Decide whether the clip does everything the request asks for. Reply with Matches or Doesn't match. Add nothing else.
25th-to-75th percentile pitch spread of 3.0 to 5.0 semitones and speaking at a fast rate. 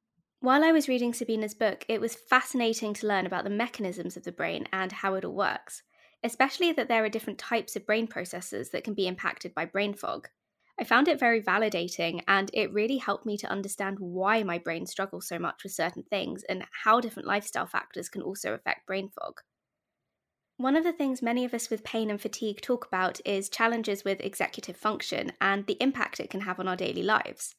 Matches